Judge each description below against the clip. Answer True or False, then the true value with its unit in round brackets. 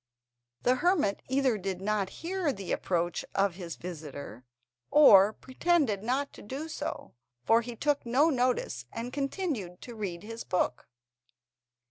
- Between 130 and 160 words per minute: True (140 wpm)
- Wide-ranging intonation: True (6.6 semitones)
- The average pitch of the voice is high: True (225 Hz)